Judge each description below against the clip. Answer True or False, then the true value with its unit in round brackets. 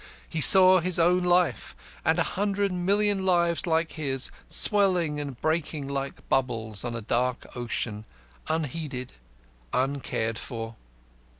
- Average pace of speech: False (125 wpm)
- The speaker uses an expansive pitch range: True (6.1 semitones)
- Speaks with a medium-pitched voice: True (155 Hz)